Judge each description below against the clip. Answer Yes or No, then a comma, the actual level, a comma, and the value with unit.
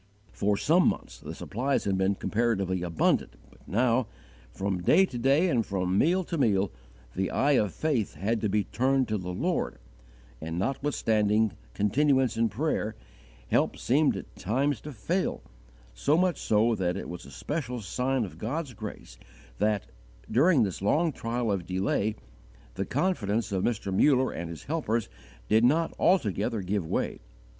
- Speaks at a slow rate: No, average, 160 wpm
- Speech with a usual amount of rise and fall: No, wide, 5.7 semitones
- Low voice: Yes, low, 110 Hz